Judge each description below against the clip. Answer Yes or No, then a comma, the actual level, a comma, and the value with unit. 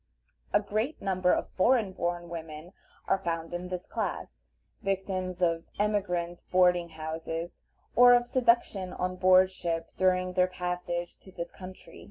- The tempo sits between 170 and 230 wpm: No, average, 145 wpm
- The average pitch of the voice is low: No, medium, 180 Hz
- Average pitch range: No, narrow, 1.8 semitones